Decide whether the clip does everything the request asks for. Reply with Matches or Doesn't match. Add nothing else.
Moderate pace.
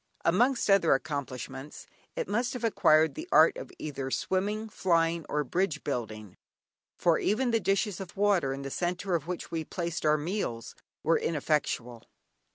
Matches